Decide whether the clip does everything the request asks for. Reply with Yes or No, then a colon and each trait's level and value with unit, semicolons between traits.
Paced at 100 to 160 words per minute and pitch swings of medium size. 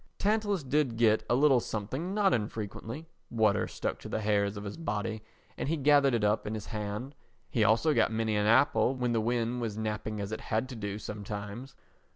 No: average, 200 wpm; average, 3.9 semitones